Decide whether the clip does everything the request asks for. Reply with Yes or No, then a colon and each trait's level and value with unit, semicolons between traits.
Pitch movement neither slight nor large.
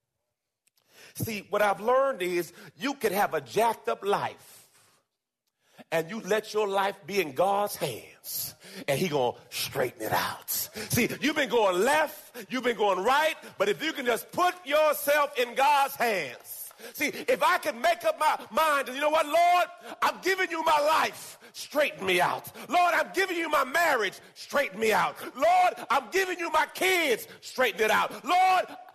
No: wide, 7.6 semitones